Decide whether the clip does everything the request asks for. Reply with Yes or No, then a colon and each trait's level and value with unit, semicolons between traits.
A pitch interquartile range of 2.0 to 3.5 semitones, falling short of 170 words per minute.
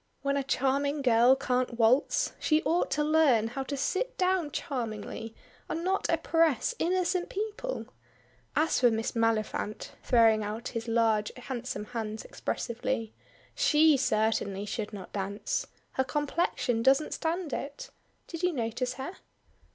No: wide, 5.6 semitones; slow, 135 wpm